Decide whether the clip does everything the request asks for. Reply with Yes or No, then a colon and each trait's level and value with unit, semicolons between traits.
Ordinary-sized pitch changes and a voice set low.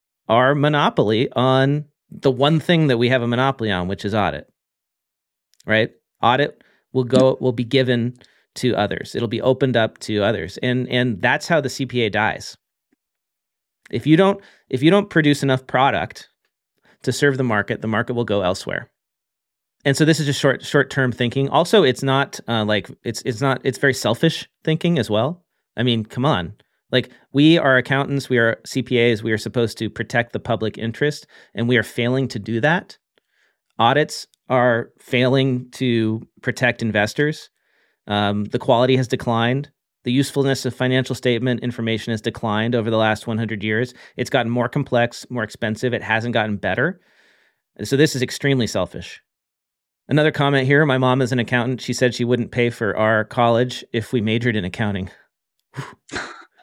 Yes: average, 3.1 semitones; low, 125 Hz